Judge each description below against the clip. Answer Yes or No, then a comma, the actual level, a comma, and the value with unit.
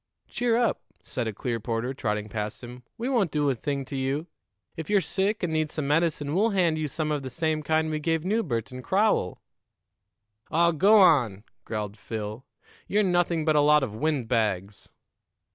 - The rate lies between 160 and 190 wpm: Yes, average, 185 wpm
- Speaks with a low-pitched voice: No, medium, 150 Hz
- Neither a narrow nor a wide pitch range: No, wide, 6.2 semitones